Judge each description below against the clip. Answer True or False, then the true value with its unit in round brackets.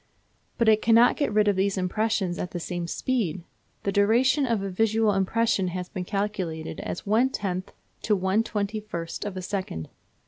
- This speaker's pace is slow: False (180 wpm)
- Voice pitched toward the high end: True (200 Hz)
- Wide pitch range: False (3.2 semitones)